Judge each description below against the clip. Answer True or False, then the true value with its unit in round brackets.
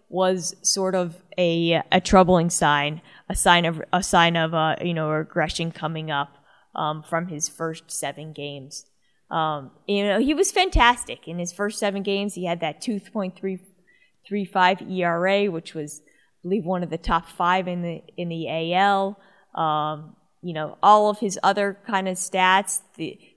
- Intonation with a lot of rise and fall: False (3.5 semitones)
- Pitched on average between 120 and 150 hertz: False (175 Hz)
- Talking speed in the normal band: True (180 wpm)